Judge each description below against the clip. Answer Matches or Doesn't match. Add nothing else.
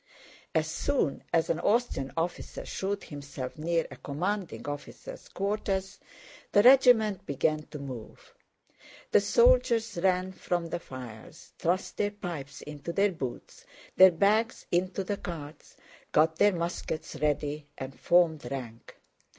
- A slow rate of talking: Matches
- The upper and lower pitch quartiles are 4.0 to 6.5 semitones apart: Matches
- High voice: Doesn't match